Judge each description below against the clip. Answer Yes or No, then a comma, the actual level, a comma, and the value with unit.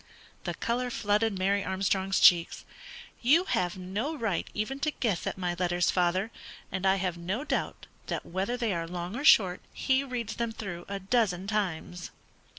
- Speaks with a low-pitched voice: No, high, 195 Hz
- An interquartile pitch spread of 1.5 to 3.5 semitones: No, average, 4.4 semitones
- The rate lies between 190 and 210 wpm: No, average, 175 wpm